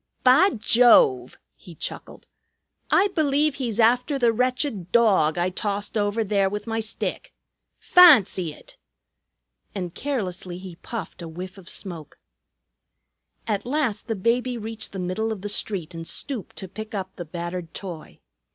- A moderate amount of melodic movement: Yes, average, 4.7 semitones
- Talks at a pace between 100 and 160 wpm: Yes, average, 150 wpm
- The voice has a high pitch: Yes, high, 205 Hz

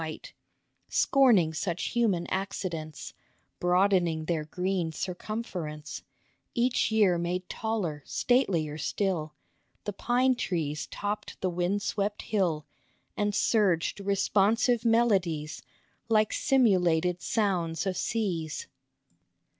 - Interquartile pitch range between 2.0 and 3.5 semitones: No, average, 4.4 semitones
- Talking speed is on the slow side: Yes, slow, 105 wpm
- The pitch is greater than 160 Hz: Yes, medium, 185 Hz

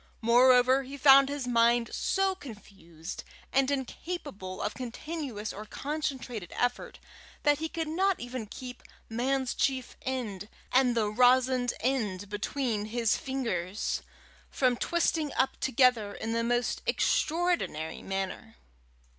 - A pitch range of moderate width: Yes, average, 3.9 semitones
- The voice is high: Yes, very high, 250 Hz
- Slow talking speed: Yes, slow, 120 wpm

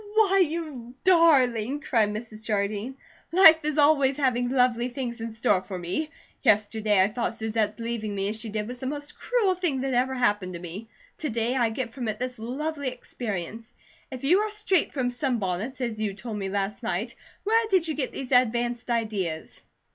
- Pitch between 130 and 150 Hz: No, high, 240 Hz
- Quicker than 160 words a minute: Yes, average, 190 wpm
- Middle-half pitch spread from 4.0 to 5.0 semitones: Yes, average, 4.7 semitones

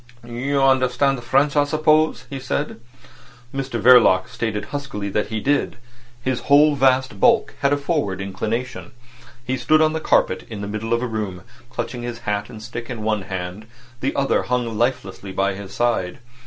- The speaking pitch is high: No, low, 120 Hz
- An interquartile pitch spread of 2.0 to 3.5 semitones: No, average, 4.7 semitones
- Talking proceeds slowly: No, average, 175 wpm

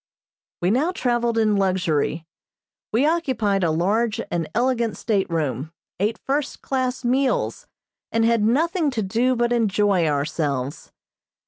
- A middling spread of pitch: No, wide, 5.9 semitones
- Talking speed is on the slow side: Yes, slow, 125 wpm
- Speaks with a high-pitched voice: Yes, high, 225 Hz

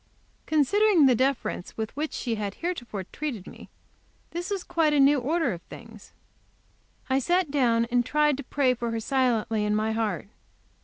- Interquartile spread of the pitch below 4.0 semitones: No, average, 5.2 semitones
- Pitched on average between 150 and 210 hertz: No, very high, 255 Hz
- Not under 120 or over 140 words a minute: No, average, 170 wpm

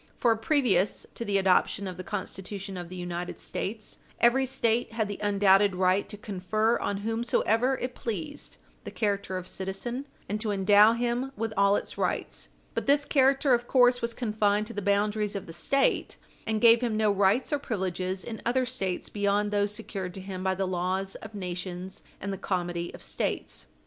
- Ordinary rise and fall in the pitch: Yes, average, 3.5 semitones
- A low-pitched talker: No, high, 205 Hz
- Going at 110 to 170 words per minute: No, average, 185 wpm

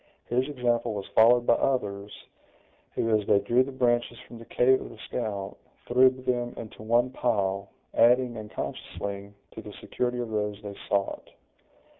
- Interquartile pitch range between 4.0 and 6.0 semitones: No, average, 3.2 semitones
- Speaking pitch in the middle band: No, low, 120 Hz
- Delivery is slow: No, average, 160 wpm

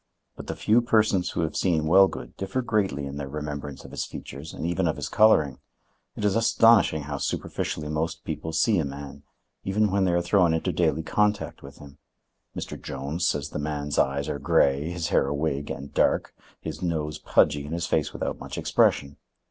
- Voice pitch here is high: No, very low, 80 Hz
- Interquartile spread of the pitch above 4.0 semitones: Yes, average, 4.8 semitones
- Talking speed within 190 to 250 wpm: Yes, average, 195 wpm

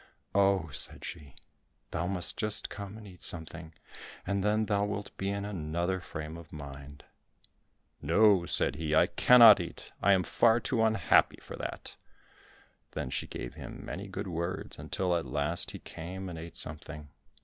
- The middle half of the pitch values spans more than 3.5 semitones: Yes, average, 4.0 semitones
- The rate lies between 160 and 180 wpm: Yes, average, 165 wpm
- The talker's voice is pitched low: Yes, very low, 90 Hz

